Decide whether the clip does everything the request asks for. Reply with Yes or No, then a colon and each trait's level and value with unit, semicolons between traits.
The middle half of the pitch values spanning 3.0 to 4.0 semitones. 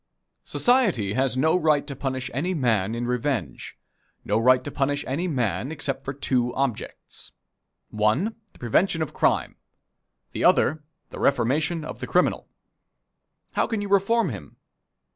No: average, 4.6 semitones